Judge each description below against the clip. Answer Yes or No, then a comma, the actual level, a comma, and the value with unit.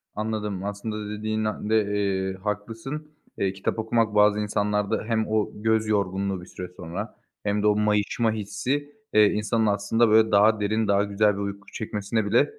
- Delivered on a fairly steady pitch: Yes, narrow, 1.4 semitones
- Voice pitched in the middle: No, low, 105 Hz